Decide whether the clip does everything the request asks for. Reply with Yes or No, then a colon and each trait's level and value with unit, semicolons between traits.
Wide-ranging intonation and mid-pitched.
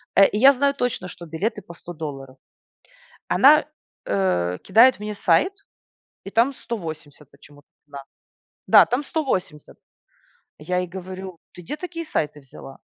Yes: wide, 7.9 semitones; medium, 180 Hz